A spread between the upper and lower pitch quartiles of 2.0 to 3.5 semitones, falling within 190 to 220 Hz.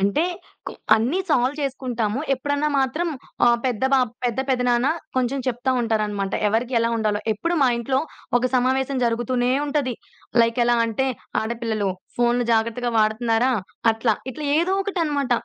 No: average, 2.8 semitones; high, 245 Hz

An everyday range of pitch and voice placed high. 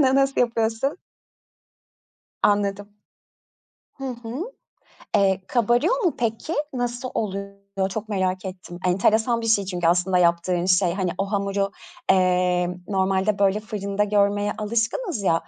Yes: average, 3.2 semitones; high, 200 Hz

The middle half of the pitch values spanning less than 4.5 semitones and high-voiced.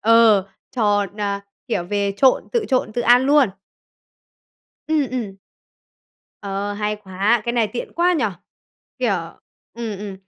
Yes: average, 3.3 semitones; high, 215 Hz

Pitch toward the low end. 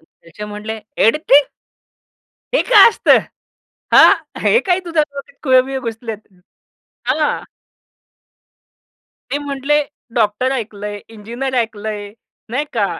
No: very high, 250 Hz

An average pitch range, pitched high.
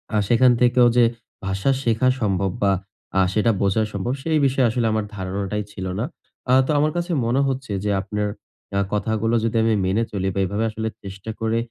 No: average, 3.4 semitones; low, 110 Hz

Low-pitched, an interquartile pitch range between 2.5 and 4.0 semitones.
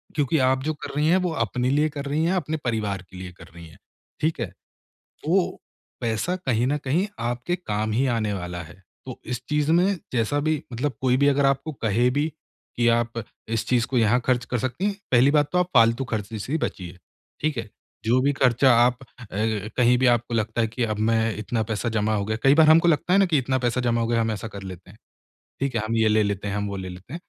No: low, 120 Hz; average, 4.7 semitones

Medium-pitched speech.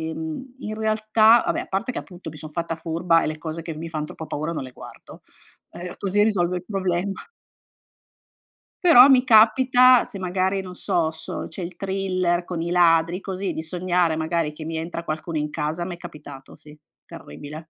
Yes: medium, 175 Hz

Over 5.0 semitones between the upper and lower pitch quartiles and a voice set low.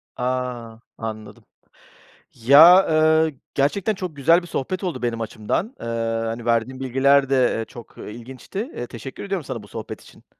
Yes: wide, 5.5 semitones; low, 130 Hz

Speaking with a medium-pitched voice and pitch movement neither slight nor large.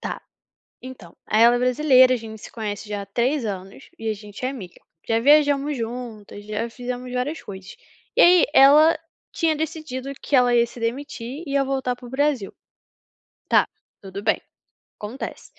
No: high, 245 Hz; average, 4.2 semitones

